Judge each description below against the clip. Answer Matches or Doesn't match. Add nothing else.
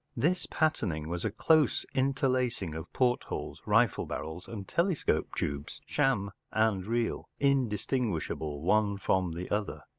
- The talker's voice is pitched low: Matches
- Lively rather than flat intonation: Matches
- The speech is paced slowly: Matches